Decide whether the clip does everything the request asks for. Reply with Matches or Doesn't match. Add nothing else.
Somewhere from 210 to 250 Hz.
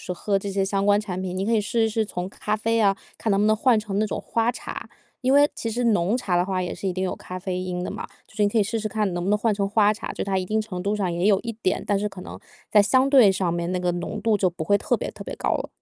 Doesn't match